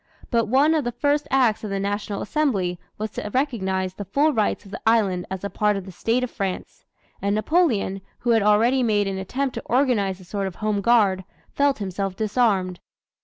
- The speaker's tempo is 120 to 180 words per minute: No, fast, 205 wpm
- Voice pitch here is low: No, high, 210 Hz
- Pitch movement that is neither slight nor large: Yes, average, 4.1 semitones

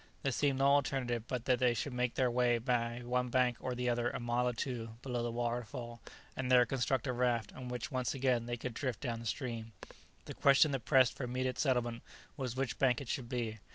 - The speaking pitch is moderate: No, low, 125 Hz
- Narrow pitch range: Yes, narrow, 1.5 semitones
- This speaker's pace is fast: Yes, fast, 225 wpm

